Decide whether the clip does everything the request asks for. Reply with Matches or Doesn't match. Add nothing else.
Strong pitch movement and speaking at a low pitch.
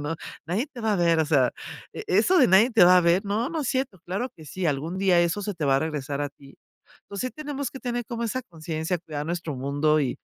Doesn't match